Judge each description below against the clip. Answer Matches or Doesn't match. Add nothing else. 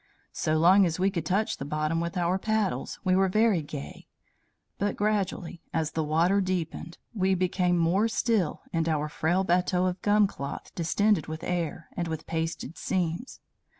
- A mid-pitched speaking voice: Matches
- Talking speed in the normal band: Matches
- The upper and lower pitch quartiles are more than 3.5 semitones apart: Doesn't match